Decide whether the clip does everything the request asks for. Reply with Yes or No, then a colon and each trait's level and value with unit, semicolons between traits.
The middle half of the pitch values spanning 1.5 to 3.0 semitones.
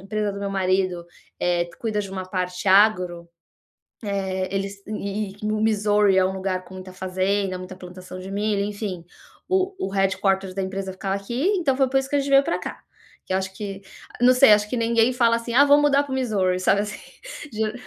Yes: narrow, 2.6 semitones